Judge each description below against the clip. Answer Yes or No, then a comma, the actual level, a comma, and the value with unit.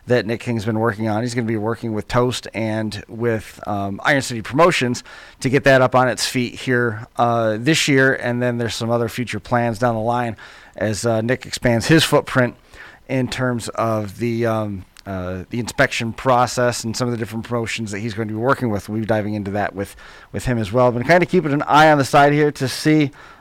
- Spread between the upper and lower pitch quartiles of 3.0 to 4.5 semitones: No, narrow, 2.5 semitones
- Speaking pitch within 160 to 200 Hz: No, low, 120 Hz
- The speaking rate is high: Yes, fast, 225 wpm